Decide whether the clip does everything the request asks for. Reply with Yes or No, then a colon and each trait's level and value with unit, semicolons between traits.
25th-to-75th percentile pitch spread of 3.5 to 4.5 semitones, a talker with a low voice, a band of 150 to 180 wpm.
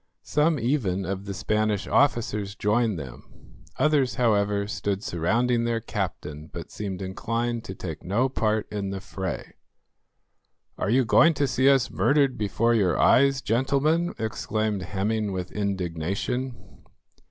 No: average, 4.2 semitones; low, 110 Hz; slow, 135 wpm